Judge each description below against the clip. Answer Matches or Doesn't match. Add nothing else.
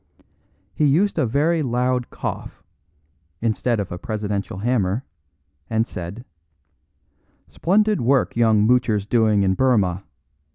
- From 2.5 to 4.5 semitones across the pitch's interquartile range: Matches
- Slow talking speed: Matches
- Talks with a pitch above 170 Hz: Doesn't match